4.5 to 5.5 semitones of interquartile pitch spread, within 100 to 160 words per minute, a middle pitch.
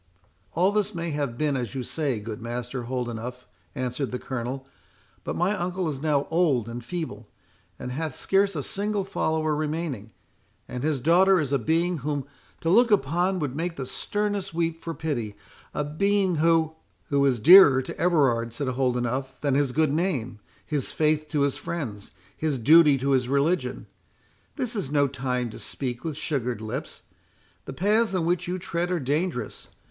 No: average, 5.1 semitones; average, 175 wpm; medium, 150 Hz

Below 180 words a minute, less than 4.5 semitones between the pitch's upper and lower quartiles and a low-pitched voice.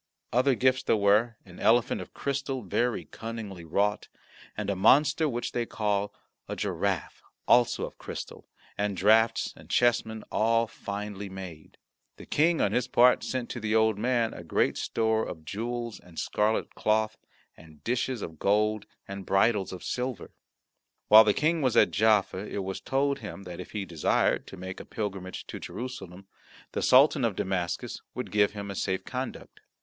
Yes: average, 170 wpm; average, 3.7 semitones; low, 110 Hz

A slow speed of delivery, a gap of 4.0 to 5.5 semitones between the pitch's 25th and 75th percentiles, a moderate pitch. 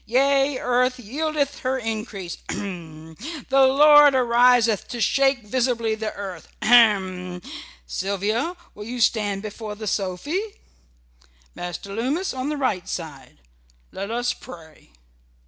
No: slow, 125 wpm; average, 4.9 semitones; high, 230 Hz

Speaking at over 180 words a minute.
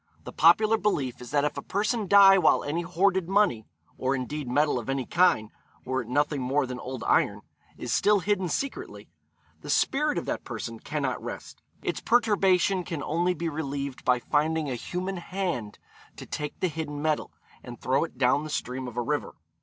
Yes: average, 190 wpm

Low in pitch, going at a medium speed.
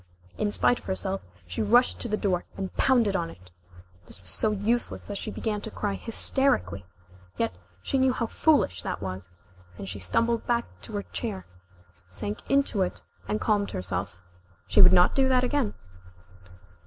No: high, 200 Hz; average, 175 wpm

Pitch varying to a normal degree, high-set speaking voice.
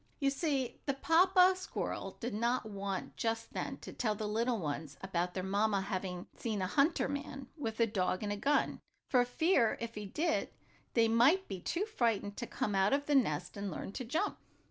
No: wide, 5.8 semitones; high, 225 Hz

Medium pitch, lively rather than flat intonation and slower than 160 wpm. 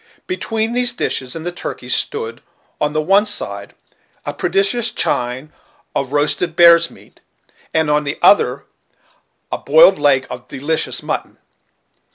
Yes: medium, 165 Hz; wide, 7.4 semitones; average, 140 wpm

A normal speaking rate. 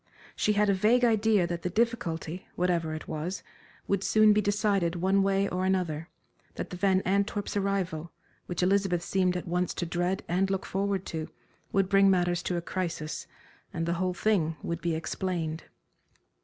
Yes: average, 175 wpm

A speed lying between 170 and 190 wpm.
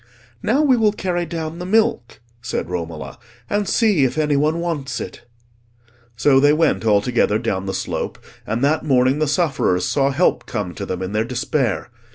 Yes: average, 185 wpm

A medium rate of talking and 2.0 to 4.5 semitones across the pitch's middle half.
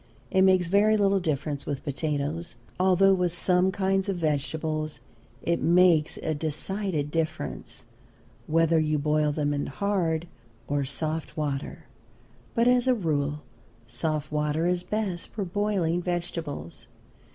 No: slow, 130 wpm; average, 3.9 semitones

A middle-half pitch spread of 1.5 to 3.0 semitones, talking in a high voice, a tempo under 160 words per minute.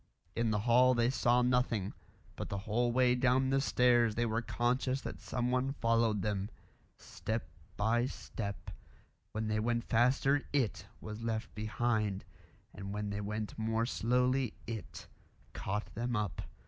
No: narrow, 2.6 semitones; low, 115 Hz; average, 150 wpm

